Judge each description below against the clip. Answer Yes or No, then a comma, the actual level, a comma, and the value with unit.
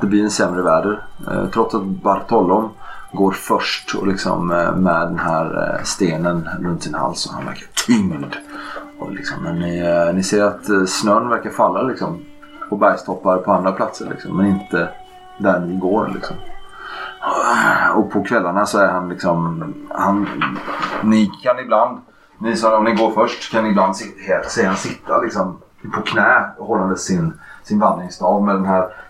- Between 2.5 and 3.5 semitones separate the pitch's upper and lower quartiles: Yes, average, 2.8 semitones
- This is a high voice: No, very low, 95 Hz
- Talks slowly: No, average, 160 wpm